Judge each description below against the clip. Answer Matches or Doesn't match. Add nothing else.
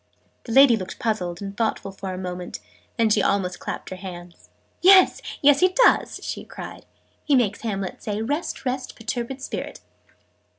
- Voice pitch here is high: Matches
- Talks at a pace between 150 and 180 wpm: Matches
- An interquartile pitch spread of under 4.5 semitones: Doesn't match